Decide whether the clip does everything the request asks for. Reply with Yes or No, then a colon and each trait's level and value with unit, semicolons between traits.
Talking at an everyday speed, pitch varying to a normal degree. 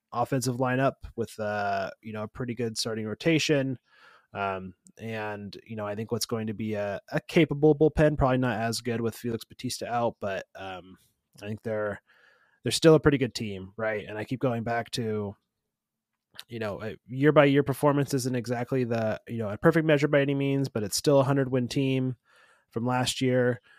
Yes: average, 195 wpm; average, 3.9 semitones